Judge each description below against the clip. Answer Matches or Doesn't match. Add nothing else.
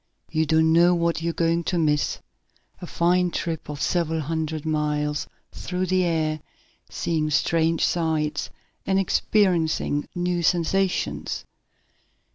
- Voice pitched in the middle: Matches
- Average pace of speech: Doesn't match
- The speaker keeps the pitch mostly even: Matches